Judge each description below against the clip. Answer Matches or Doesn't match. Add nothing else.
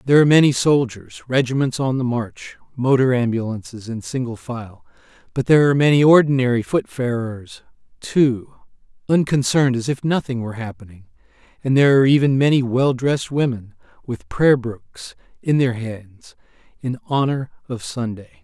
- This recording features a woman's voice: Doesn't match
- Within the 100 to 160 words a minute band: Matches